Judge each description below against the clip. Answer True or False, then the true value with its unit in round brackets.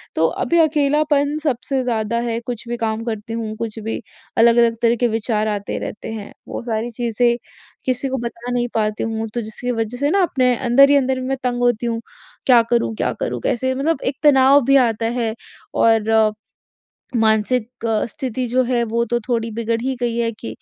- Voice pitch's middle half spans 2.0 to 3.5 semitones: True (2.5 semitones)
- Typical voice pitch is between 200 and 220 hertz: False (235 Hz)